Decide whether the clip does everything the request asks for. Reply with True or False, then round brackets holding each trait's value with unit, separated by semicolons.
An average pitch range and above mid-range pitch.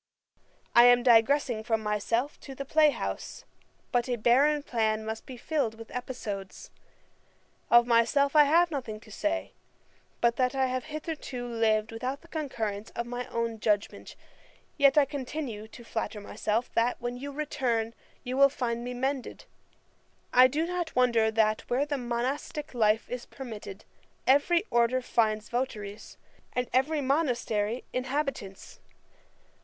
True (3.7 semitones; 245 Hz)